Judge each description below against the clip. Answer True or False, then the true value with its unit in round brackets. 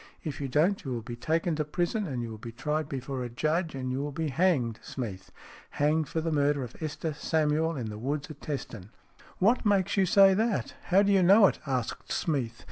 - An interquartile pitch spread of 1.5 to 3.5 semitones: False (5.1 semitones)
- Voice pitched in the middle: True (150 Hz)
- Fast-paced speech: True (225 wpm)